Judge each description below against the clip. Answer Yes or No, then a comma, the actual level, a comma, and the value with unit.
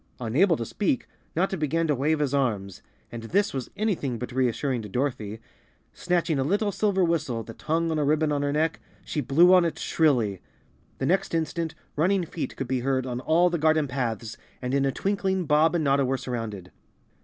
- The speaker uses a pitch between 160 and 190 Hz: No, medium, 145 Hz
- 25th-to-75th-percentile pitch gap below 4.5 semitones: No, average, 5.0 semitones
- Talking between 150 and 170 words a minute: No, average, 200 wpm